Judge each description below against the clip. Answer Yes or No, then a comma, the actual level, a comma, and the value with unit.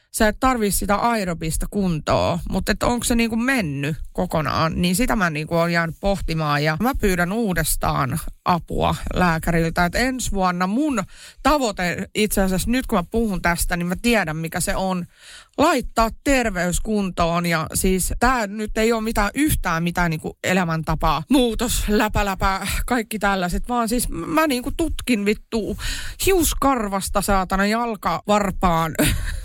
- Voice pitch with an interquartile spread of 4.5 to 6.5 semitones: Yes, average, 4.8 semitones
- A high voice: Yes, high, 200 Hz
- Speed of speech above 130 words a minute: Yes, average, 145 wpm